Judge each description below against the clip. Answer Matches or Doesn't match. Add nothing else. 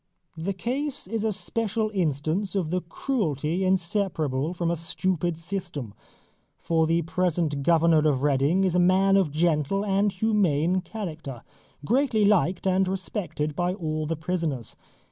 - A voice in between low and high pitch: Matches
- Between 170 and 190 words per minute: Doesn't match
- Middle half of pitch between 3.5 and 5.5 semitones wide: Matches